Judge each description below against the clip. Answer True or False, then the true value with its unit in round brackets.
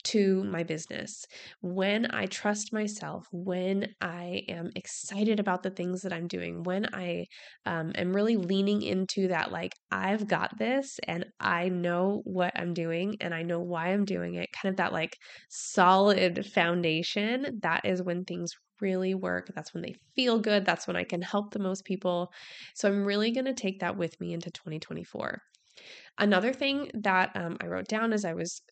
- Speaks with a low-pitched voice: False (185 Hz)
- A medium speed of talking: True (180 wpm)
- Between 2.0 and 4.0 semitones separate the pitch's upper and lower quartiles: True (2.9 semitones)